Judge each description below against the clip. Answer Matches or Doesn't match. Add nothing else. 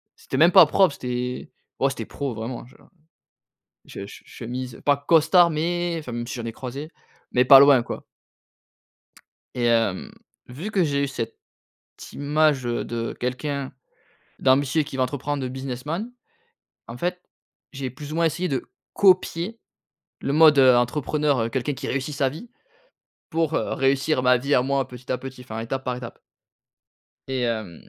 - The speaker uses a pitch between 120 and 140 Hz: Matches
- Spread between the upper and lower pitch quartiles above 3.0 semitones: Matches